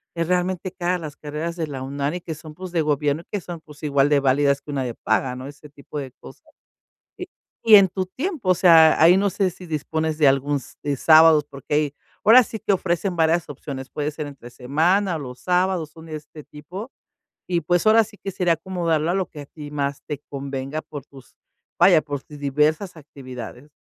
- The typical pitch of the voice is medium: Yes, medium, 155 Hz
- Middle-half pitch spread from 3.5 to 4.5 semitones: Yes, average, 3.8 semitones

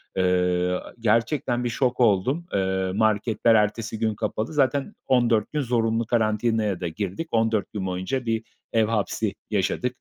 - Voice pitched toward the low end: Yes, low, 110 Hz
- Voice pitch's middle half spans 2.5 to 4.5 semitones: Yes, average, 3.1 semitones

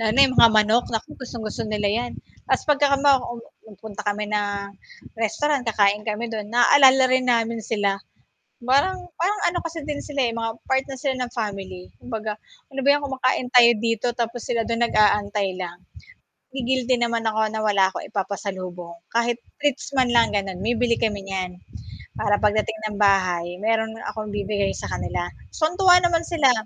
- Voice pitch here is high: Yes, high, 225 Hz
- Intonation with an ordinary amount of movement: Yes, average, 3.9 semitones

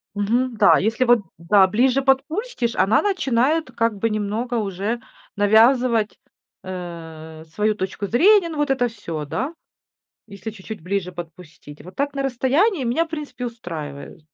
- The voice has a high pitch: Yes, high, 225 Hz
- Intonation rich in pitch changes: Yes, wide, 5.8 semitones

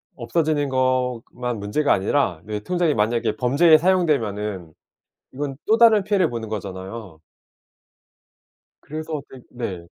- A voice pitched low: Yes, low, 125 Hz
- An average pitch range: No, wide, 6.7 semitones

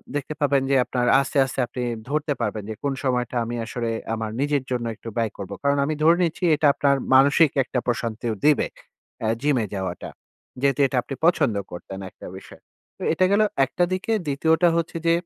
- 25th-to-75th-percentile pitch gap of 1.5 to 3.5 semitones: No, average, 4.2 semitones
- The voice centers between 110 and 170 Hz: Yes, low, 135 Hz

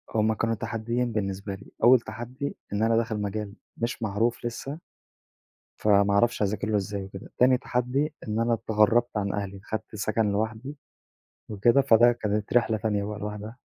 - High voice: No, low, 110 Hz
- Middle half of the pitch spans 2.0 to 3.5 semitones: Yes, narrow, 2.4 semitones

